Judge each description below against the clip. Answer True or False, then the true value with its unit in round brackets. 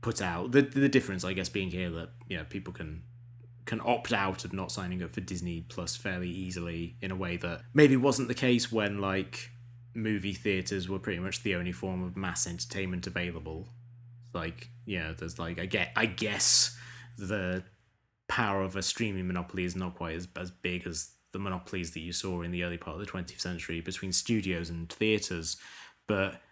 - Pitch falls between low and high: False (95 Hz)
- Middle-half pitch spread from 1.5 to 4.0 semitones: False (4.4 semitones)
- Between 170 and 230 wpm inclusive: True (200 wpm)